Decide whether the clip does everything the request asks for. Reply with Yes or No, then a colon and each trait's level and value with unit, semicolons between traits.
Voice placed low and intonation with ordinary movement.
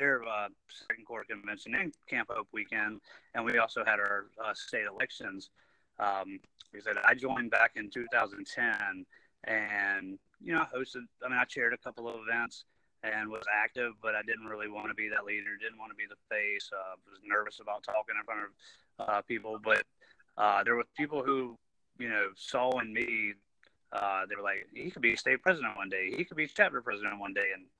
No: low, 115 Hz; wide, 5.7 semitones